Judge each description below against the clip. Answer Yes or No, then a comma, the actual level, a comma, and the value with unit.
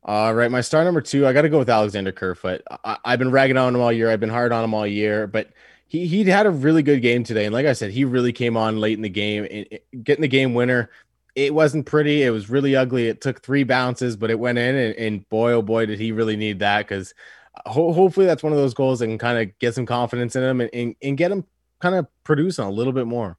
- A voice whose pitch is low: Yes, low, 120 Hz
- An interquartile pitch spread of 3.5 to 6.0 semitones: Yes, average, 3.9 semitones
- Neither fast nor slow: No, fast, 275 wpm